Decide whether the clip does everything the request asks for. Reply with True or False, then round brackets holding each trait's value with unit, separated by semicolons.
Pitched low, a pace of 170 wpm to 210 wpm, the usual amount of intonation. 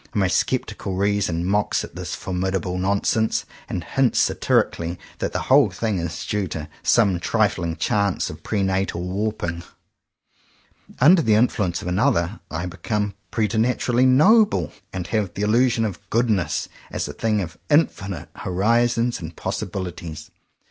False (100 Hz; 140 wpm; 4.1 semitones)